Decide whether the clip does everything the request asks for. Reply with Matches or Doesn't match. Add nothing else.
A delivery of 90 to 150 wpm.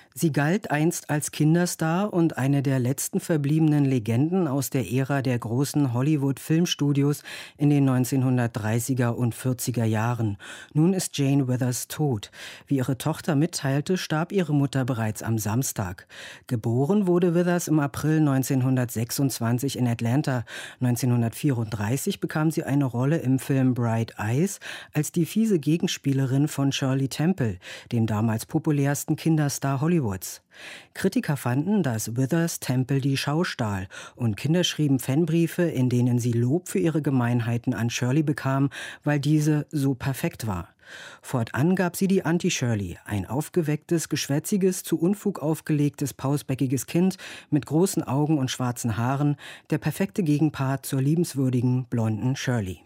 Matches